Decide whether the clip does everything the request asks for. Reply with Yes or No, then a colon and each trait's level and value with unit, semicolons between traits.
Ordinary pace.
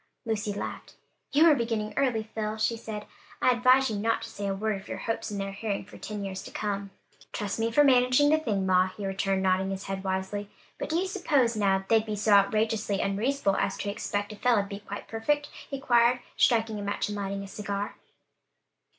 No: fast, 220 wpm